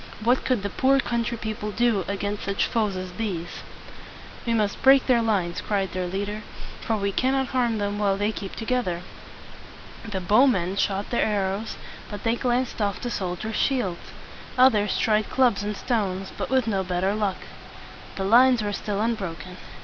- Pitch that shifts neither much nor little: Yes, average, 3.4 semitones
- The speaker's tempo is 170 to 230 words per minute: Yes, average, 180 wpm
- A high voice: Yes, high, 210 Hz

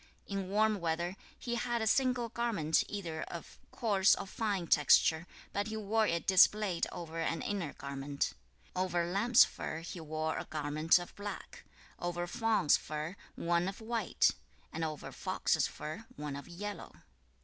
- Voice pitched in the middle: Yes, medium, 180 Hz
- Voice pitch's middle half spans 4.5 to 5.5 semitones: Yes, average, 4.8 semitones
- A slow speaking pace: No, average, 160 wpm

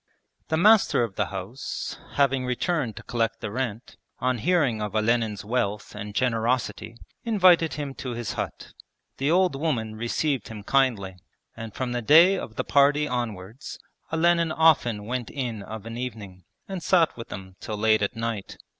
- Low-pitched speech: Yes, low, 120 Hz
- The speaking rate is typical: Yes, average, 165 wpm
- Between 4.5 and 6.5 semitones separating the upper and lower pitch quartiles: Yes, average, 5.0 semitones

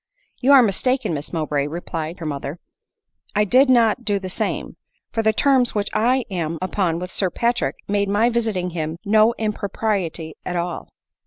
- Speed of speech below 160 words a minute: No, average, 180 wpm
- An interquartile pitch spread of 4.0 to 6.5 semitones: Yes, average, 5.0 semitones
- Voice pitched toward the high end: Yes, high, 200 Hz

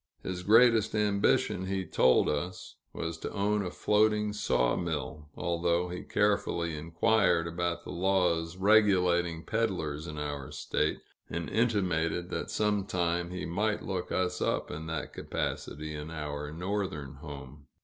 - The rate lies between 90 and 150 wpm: Yes, slow, 135 wpm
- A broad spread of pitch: No, average, 4.0 semitones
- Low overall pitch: Yes, very low, 85 Hz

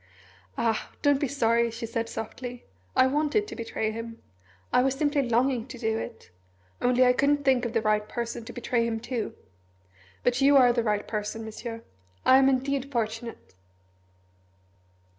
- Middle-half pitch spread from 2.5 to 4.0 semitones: Yes, average, 2.8 semitones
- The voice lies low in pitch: No, high, 240 Hz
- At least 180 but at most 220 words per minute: No, average, 165 wpm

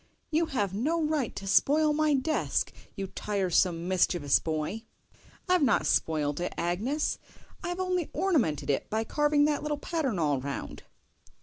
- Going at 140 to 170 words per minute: Yes, average, 145 wpm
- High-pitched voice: Yes, high, 240 Hz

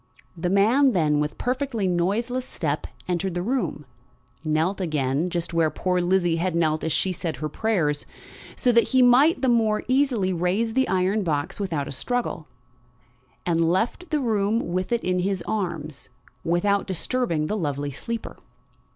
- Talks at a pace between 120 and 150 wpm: No, average, 160 wpm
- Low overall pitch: No, medium, 185 Hz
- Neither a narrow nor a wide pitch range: No, wide, 5.7 semitones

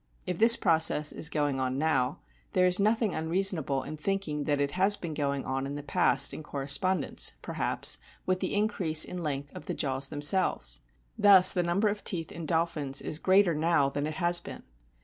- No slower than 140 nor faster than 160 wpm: No, average, 195 wpm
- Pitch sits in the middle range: Yes, medium, 160 Hz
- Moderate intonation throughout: Yes, average, 4.4 semitones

